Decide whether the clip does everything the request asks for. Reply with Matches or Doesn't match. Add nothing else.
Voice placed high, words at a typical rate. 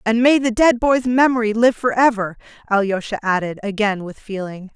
Matches